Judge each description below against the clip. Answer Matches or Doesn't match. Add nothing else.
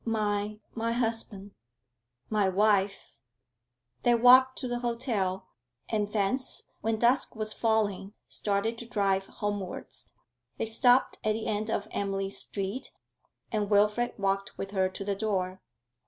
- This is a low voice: Doesn't match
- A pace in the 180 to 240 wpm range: Doesn't match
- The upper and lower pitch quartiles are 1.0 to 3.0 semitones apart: Matches